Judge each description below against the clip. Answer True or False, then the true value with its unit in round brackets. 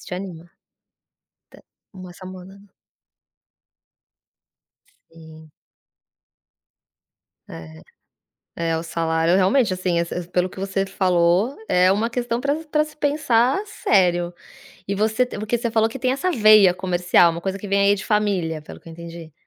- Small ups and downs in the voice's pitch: False (4.4 semitones)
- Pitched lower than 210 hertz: True (190 Hz)